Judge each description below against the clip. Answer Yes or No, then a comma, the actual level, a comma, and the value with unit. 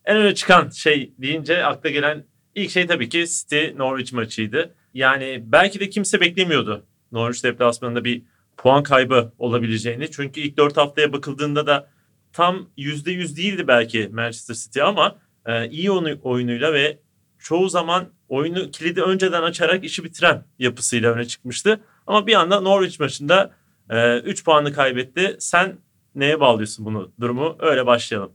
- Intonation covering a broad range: Yes, wide, 6.1 semitones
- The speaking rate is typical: No, fast, 145 wpm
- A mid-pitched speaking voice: Yes, medium, 145 Hz